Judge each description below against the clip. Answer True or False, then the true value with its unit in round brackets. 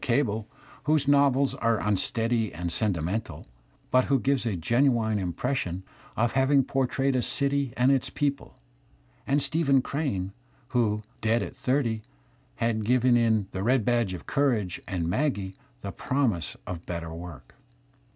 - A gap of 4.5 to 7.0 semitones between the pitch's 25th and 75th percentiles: True (5.4 semitones)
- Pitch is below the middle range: True (115 Hz)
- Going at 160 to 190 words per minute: False (145 wpm)